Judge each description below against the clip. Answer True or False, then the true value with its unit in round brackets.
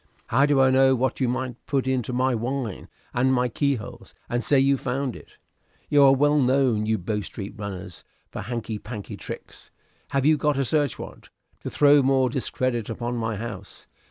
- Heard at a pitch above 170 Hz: False (130 Hz)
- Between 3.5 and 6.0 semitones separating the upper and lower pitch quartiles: False (3.1 semitones)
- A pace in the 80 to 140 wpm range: False (190 wpm)